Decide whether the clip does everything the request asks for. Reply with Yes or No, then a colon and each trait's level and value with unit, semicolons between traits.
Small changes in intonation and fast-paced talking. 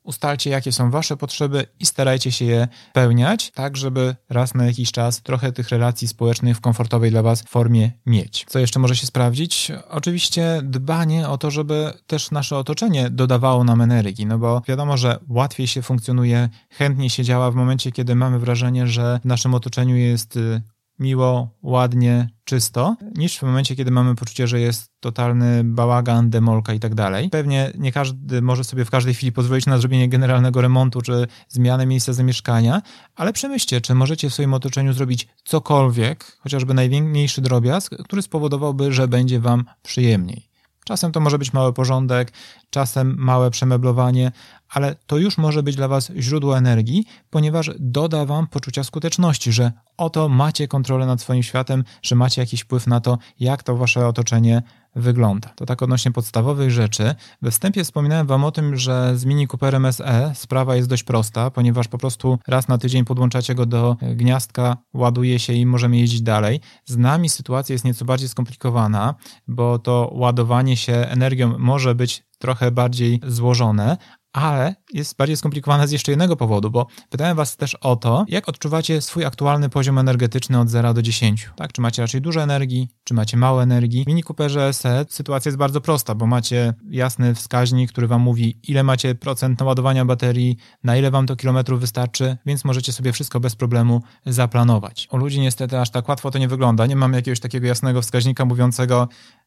Yes: narrow, 2.2 semitones; fast, 175 wpm